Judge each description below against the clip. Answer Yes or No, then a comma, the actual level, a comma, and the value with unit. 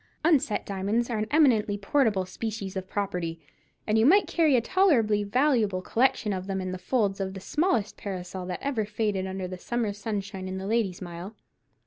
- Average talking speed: Yes, average, 185 wpm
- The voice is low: No, high, 205 Hz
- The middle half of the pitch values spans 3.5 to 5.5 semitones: Yes, average, 3.8 semitones